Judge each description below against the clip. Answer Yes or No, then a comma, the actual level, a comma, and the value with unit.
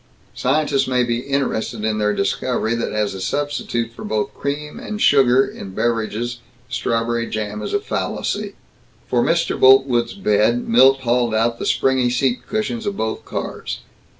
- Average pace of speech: Yes, average, 155 wpm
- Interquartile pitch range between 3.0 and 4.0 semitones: Yes, average, 3.3 semitones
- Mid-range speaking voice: No, low, 120 Hz